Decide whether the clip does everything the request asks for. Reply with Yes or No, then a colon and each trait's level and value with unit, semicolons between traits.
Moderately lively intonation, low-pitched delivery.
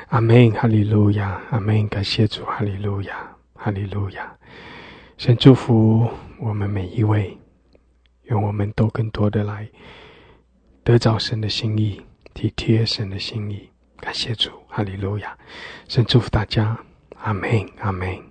No: narrow, 2.1 semitones; low, 105 Hz